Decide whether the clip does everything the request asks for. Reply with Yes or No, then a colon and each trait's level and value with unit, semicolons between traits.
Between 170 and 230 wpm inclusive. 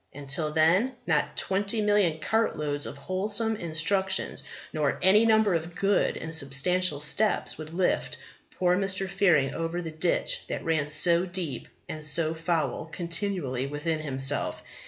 No: average, 150 wpm